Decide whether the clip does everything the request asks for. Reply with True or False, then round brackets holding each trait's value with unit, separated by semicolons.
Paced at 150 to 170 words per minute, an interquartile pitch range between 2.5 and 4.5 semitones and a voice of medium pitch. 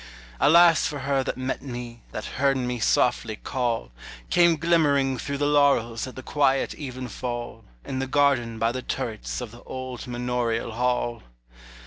False (155 wpm; 2.9 semitones; 130 Hz)